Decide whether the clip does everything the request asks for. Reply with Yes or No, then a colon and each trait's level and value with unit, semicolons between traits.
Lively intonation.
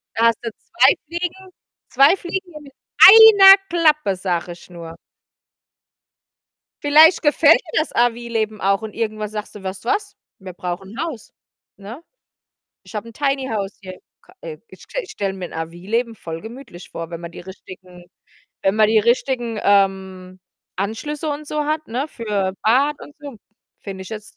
Yes: wide, 7.4 semitones